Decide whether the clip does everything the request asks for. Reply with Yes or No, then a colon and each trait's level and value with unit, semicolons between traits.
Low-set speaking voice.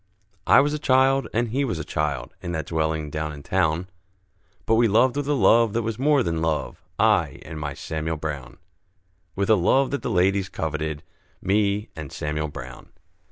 Yes: very low, 90 Hz